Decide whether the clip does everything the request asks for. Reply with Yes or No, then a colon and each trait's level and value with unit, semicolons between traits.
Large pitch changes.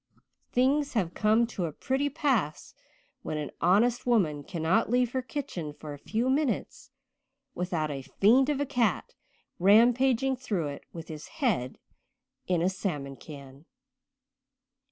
Yes: wide, 8.2 semitones